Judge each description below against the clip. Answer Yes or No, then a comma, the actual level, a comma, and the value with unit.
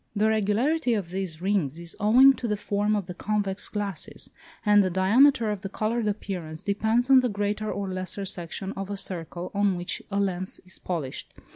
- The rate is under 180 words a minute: No, average, 190 wpm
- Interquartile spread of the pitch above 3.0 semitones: No, narrow, 2.5 semitones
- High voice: Yes, high, 200 Hz